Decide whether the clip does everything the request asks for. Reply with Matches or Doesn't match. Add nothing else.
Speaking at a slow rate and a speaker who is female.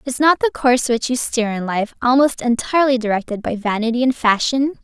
Doesn't match